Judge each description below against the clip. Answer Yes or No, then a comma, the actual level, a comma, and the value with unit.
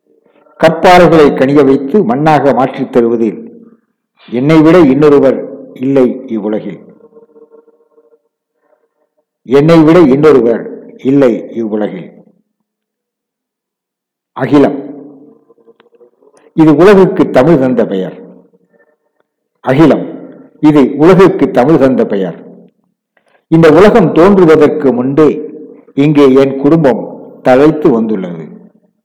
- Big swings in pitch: Yes, wide, 8.1 semitones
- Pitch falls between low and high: Yes, medium, 155 Hz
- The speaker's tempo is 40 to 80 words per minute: Yes, slow, 75 wpm